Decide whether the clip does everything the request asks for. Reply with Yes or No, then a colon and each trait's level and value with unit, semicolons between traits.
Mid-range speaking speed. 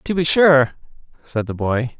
Yes: average, 180 wpm